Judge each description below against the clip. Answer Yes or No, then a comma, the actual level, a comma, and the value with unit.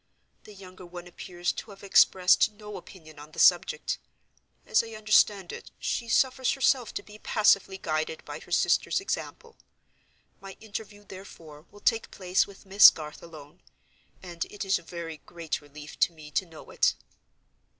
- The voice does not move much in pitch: No, average, 4.2 semitones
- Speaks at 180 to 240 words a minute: No, average, 160 wpm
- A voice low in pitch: No, high, 190 Hz